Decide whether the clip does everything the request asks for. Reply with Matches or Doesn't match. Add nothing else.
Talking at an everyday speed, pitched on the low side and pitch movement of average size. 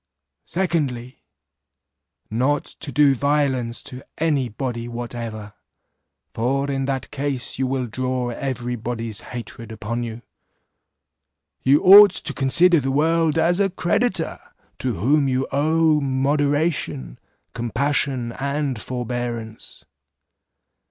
Doesn't match